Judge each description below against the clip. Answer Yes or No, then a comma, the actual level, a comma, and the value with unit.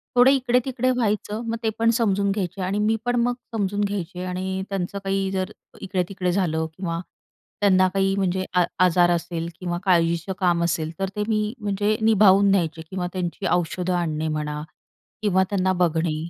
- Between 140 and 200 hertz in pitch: Yes, high, 190 Hz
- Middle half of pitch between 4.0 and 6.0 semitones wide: No, average, 2.8 semitones